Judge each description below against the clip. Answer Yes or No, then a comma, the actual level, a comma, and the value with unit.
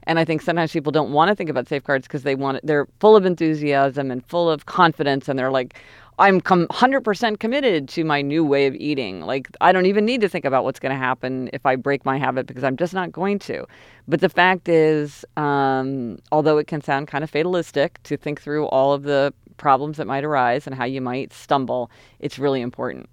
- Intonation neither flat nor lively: Yes, average, 3.7 semitones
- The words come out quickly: Yes, fast, 225 wpm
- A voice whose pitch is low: No, medium, 145 Hz